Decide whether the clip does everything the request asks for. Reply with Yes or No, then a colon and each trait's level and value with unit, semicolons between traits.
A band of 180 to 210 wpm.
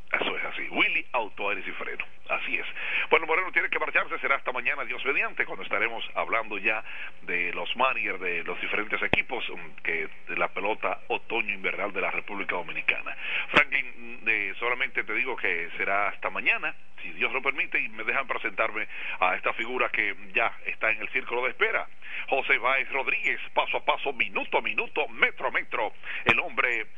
Yes: average, 185 wpm